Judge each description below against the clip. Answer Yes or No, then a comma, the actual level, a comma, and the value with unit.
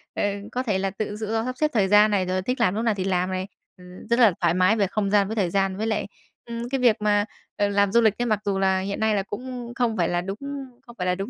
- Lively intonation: No, average, 3.1 semitones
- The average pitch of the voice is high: Yes, high, 205 Hz